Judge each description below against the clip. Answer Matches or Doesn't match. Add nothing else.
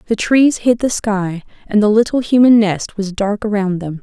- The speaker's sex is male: Doesn't match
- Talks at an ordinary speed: Doesn't match